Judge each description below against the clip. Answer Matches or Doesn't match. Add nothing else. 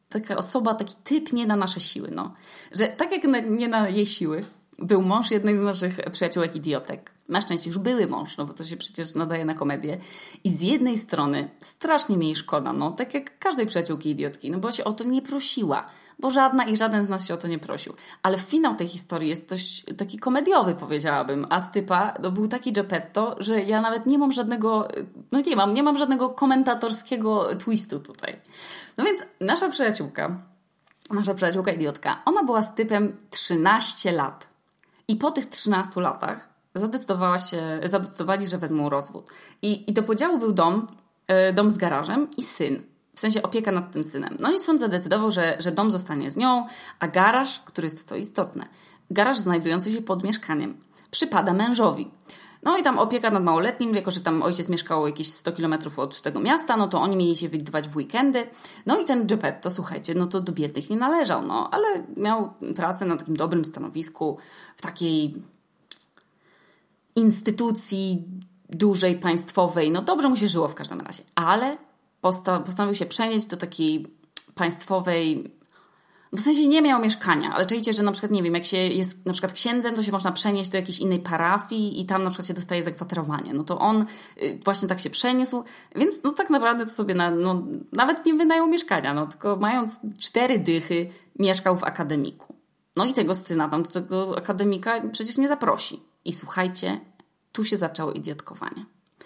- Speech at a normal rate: Doesn't match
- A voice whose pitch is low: Doesn't match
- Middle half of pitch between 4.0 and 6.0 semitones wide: Matches